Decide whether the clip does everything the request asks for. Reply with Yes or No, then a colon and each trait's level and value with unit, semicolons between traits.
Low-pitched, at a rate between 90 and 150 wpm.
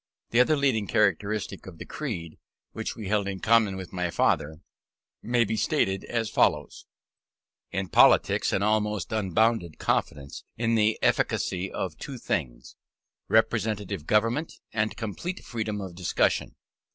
Yes: low, 105 Hz; average, 140 wpm